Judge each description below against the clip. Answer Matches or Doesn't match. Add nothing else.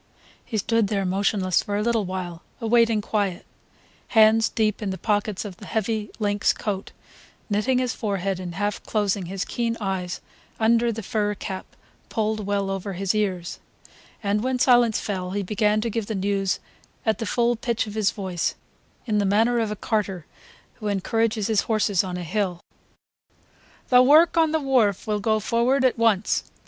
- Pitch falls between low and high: Doesn't match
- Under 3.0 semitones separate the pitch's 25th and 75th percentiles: Matches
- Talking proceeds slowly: Doesn't match